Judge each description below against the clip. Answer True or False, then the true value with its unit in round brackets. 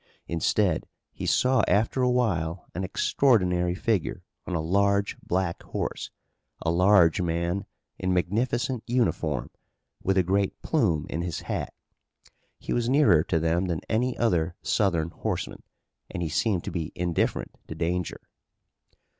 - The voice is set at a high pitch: False (90 Hz)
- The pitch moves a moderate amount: True (4.3 semitones)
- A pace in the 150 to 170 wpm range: False (140 wpm)